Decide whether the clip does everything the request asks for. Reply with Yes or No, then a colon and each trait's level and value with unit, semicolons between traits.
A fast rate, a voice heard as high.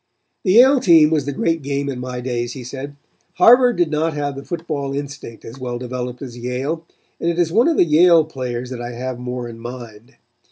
No: fast, 210 wpm; medium, 140 Hz